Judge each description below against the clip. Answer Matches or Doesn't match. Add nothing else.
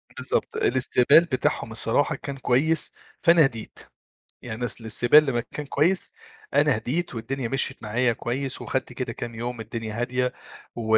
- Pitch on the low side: Matches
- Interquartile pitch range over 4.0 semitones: Doesn't match